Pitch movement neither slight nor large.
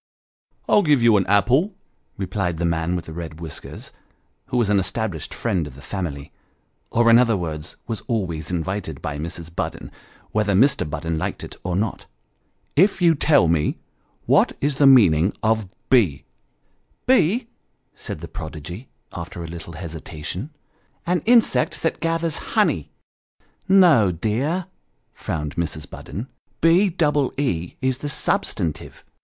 No: wide, 8.9 semitones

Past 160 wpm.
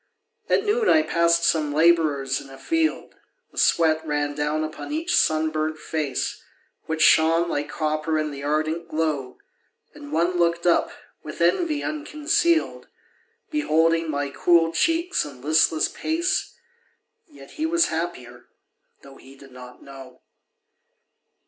No: slow, 135 wpm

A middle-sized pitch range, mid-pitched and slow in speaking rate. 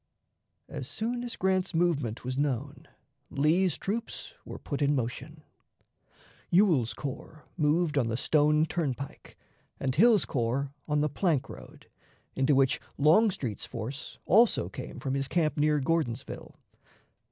Yes: average, 4.2 semitones; medium, 150 Hz; slow, 130 wpm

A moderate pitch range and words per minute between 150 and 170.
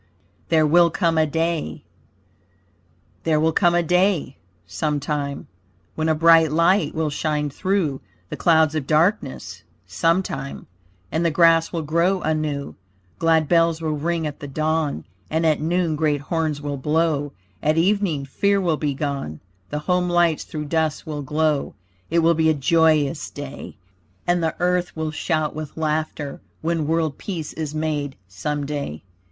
No: narrow, 2.1 semitones; average, 155 wpm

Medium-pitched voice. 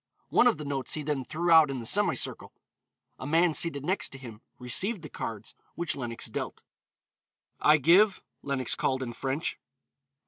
Yes: medium, 145 Hz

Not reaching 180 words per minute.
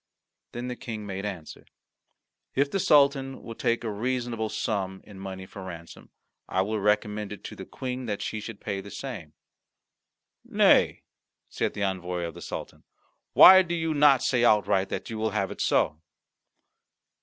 Yes: average, 170 wpm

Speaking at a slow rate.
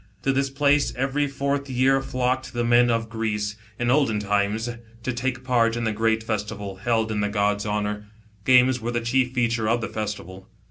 No: average, 190 wpm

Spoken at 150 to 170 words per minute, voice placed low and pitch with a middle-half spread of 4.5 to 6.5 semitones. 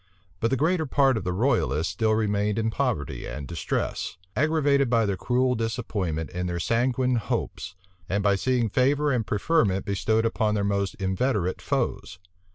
Yes: average, 165 wpm; low, 110 Hz; average, 5.0 semitones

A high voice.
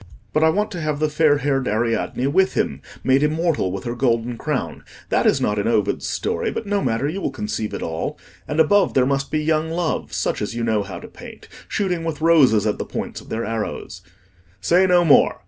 No: medium, 140 Hz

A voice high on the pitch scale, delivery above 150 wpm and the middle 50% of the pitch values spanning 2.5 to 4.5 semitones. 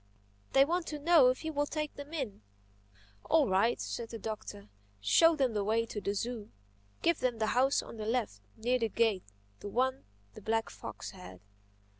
No: high, 235 Hz; average, 185 wpm; average, 5.1 semitones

